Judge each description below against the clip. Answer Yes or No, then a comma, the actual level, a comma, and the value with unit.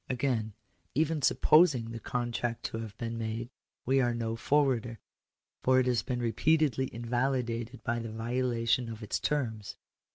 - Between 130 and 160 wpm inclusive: Yes, average, 150 wpm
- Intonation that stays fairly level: Yes, narrow, 2.2 semitones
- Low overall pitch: Yes, low, 120 Hz